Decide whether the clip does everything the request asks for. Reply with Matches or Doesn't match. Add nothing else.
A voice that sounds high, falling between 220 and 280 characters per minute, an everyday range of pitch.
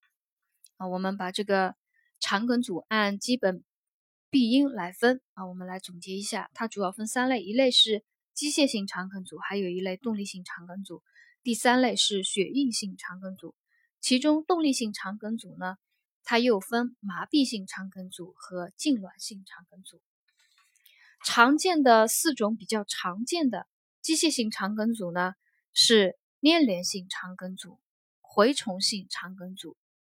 Matches